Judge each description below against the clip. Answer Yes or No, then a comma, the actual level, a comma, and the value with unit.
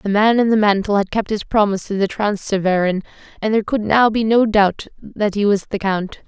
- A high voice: Yes, high, 205 Hz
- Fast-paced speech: Yes, fast, 230 wpm